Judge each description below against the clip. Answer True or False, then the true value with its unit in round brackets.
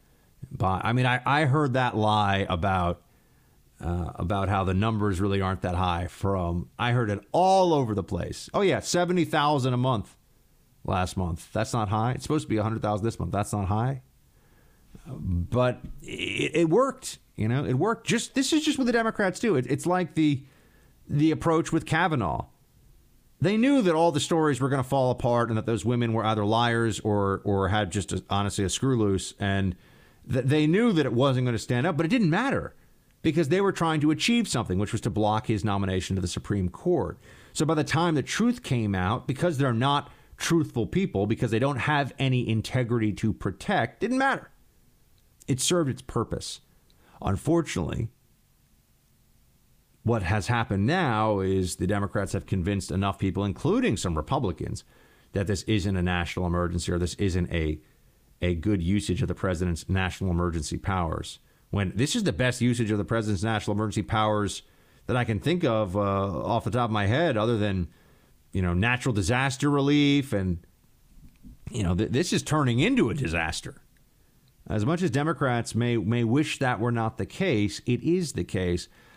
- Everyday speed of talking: True (190 wpm)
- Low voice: True (115 Hz)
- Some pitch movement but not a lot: False (6.2 semitones)